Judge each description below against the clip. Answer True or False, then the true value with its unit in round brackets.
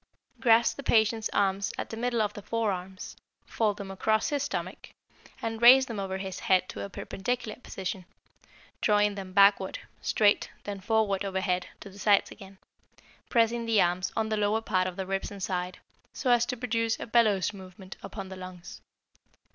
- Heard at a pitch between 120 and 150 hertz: False (205 Hz)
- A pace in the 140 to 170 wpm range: False (180 wpm)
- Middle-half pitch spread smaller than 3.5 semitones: True (2.9 semitones)